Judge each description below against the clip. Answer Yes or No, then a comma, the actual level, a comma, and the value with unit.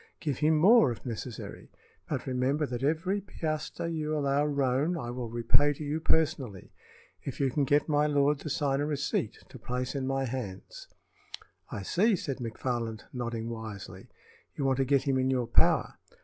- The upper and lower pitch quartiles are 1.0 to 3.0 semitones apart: No, average, 3.4 semitones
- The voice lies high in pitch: No, low, 135 Hz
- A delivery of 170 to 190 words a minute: Yes, average, 175 wpm